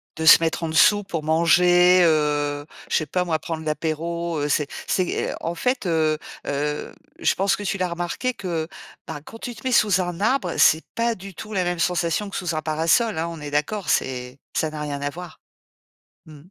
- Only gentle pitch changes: No, average, 3.1 semitones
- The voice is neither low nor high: Yes, medium, 165 Hz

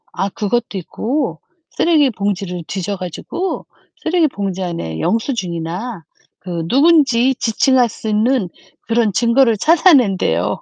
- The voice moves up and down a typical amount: No, wide, 6.2 semitones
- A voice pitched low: No, high, 220 Hz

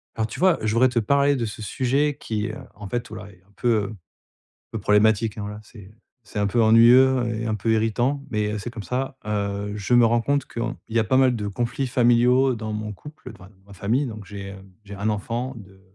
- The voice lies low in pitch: Yes, low, 110 Hz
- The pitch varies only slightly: No, average, 3.0 semitones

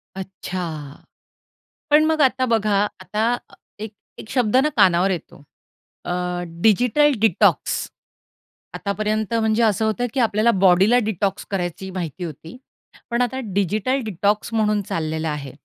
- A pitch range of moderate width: Yes, average, 4.0 semitones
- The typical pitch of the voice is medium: No, high, 210 Hz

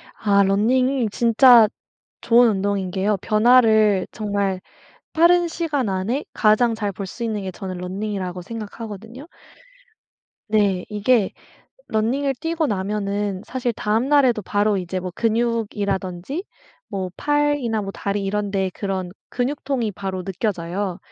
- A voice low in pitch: No, high, 210 Hz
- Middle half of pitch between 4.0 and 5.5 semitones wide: No, average, 3.6 semitones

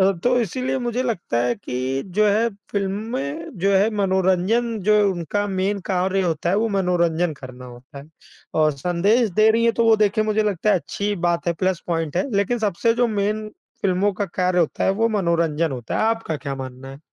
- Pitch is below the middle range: No, high, 190 Hz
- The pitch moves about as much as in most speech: Yes, average, 4.2 semitones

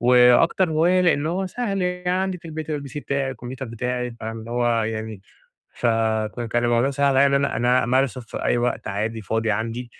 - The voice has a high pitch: No, low, 125 Hz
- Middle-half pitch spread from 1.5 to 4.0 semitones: No, average, 4.7 semitones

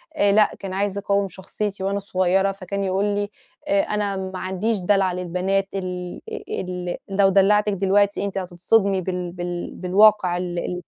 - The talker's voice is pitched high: Yes, high, 195 Hz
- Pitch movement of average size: No, narrow, 1.7 semitones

